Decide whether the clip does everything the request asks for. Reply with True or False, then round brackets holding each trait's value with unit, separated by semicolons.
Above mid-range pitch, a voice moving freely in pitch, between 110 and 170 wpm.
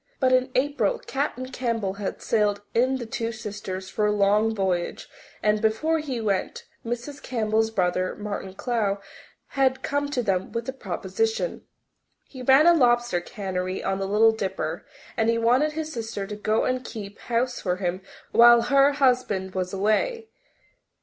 False (225 Hz; 4.3 semitones; 165 wpm)